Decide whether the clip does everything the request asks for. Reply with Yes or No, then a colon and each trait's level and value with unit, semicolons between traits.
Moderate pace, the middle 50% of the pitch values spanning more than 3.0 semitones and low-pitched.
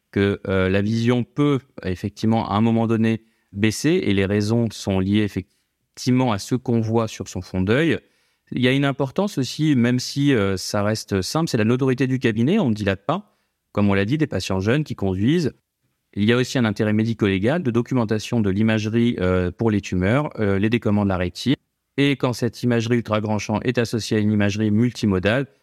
Yes: average, 205 wpm; average, 3.5 semitones; low, 115 Hz